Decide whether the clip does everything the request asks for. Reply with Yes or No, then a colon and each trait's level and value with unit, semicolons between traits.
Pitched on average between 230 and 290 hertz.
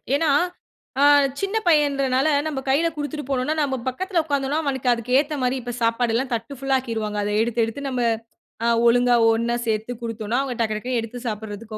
Yes: very high, 250 Hz